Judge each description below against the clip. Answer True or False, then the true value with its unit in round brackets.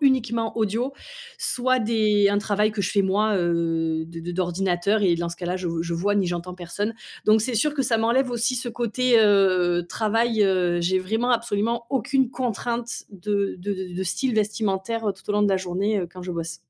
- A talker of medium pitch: False (205 Hz)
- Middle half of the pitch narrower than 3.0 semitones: False (4.2 semitones)